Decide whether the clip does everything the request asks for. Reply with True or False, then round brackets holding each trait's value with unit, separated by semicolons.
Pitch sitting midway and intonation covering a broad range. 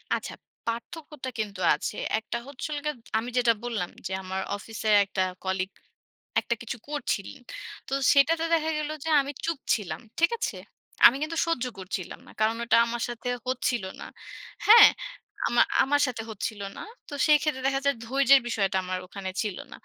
False (240 Hz; 5.7 semitones)